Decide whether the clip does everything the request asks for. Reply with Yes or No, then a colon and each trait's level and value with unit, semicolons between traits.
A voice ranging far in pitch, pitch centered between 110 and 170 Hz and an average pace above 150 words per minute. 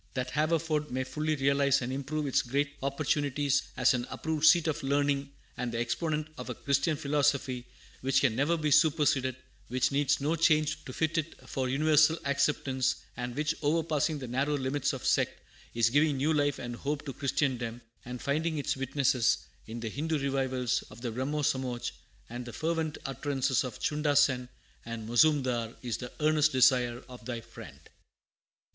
No: average, 3.0 semitones; medium, 140 Hz; average, 170 wpm